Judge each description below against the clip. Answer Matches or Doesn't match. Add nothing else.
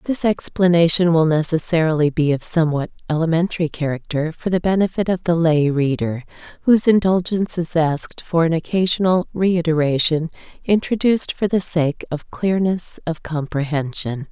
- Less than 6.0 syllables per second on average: Matches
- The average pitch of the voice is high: Doesn't match